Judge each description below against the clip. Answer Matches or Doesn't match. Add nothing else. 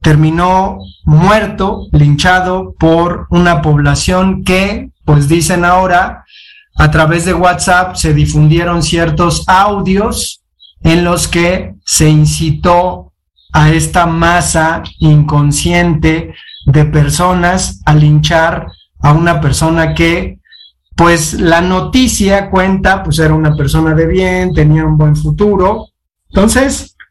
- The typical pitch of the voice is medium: Matches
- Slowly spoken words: Matches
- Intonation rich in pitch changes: Doesn't match